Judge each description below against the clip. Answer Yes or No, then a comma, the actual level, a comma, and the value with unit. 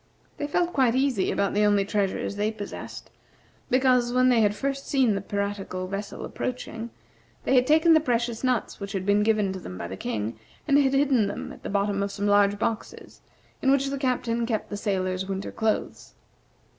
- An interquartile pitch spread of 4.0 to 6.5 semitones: Yes, average, 4.3 semitones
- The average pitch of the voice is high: Yes, high, 215 Hz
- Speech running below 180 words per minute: No, average, 195 wpm